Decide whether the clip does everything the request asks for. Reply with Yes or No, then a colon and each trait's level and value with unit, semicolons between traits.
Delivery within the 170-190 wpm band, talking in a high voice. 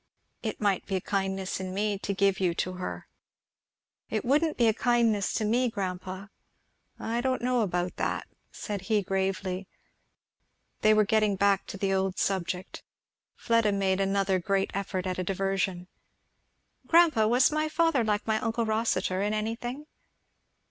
No: average, 160 wpm; high, 200 Hz